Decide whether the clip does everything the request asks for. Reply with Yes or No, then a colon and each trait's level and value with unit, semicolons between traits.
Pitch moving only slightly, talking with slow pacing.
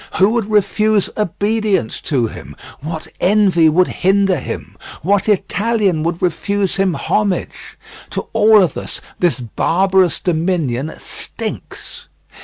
No: average, 3.7 semitones; slow, 120 wpm